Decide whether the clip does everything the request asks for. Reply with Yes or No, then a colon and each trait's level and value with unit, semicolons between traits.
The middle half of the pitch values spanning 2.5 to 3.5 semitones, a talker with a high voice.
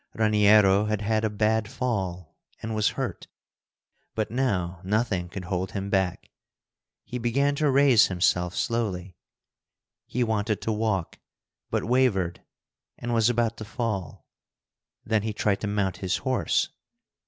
No: average, 3.2 semitones; low, 105 Hz